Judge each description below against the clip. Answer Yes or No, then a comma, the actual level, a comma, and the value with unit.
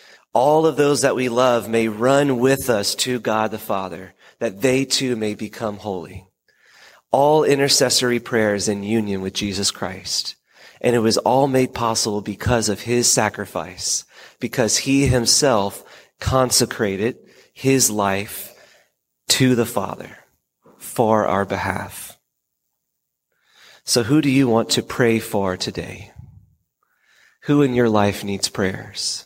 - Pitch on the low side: Yes, low, 115 Hz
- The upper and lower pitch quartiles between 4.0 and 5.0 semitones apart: Yes, average, 4.3 semitones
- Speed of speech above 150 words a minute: No, slow, 135 wpm